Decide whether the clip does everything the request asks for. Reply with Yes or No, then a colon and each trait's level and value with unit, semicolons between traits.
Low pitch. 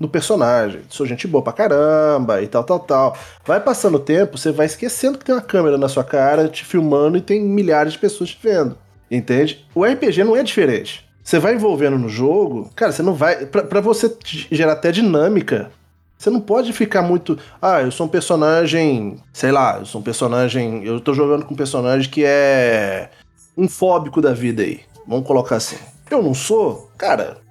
No: medium, 155 Hz